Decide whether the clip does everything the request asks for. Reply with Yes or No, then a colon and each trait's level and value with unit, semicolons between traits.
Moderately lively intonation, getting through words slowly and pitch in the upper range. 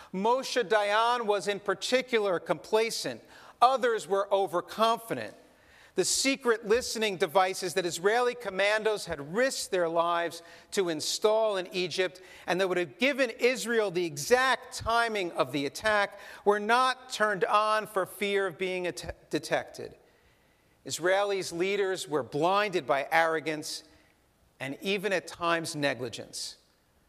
Yes: average, 4.6 semitones; slow, 125 wpm; high, 195 Hz